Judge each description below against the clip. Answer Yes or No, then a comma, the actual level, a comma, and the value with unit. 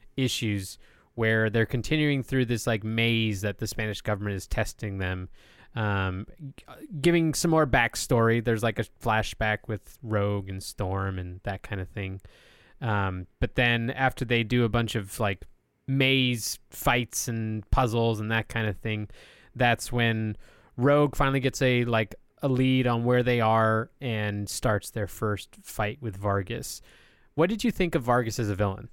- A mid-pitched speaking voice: No, low, 115 Hz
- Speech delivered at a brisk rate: No, average, 170 wpm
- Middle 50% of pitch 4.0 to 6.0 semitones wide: No, average, 3.2 semitones